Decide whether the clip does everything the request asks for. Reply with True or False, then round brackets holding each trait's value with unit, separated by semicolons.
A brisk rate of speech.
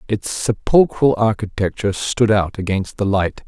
False (140 wpm)